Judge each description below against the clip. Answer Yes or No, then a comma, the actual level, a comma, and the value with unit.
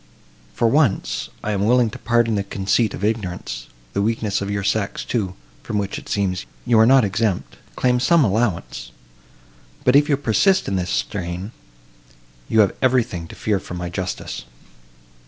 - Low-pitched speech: Yes, low, 100 Hz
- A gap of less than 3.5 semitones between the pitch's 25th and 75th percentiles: No, average, 4.6 semitones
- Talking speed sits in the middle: Yes, average, 165 wpm